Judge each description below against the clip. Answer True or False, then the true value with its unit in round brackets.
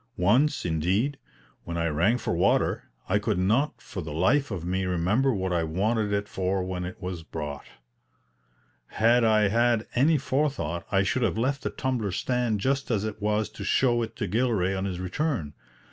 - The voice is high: False (105 Hz)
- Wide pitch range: False (4.9 semitones)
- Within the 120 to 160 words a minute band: False (185 wpm)